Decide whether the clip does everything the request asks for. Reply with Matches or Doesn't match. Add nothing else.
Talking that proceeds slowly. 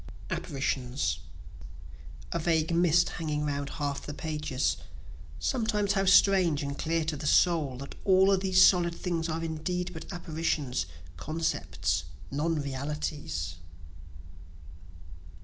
Matches